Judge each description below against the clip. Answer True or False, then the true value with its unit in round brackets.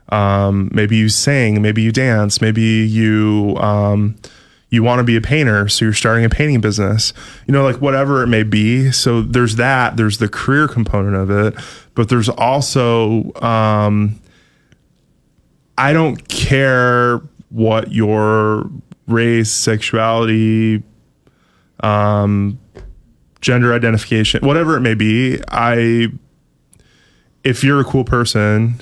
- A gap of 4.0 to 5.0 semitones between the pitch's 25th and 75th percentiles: False (2.9 semitones)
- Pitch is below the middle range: True (115 Hz)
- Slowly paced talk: True (130 wpm)